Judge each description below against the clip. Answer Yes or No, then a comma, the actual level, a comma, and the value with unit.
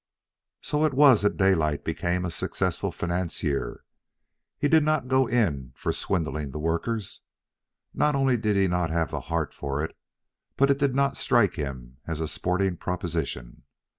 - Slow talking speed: No, average, 165 wpm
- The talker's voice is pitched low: Yes, very low, 90 Hz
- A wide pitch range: Yes, wide, 8.2 semitones